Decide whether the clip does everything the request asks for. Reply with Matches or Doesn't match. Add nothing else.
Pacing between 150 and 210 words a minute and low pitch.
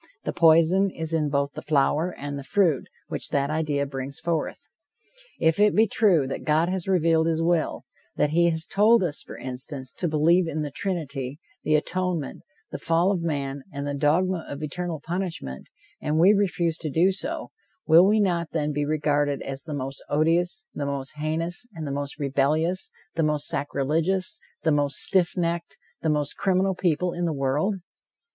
Doesn't match